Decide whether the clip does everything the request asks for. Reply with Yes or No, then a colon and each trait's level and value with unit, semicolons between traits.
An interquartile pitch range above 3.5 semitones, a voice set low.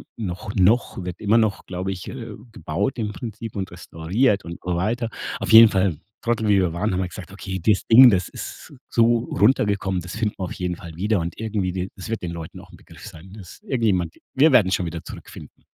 Yes: average, 3.9 semitones; very low, 95 Hz